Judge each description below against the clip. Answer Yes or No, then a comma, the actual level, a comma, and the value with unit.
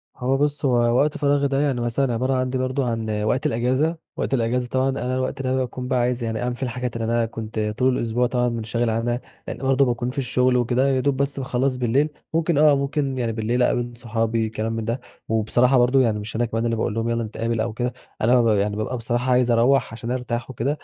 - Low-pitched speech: Yes, low, 125 Hz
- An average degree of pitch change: No, narrow, 2.2 semitones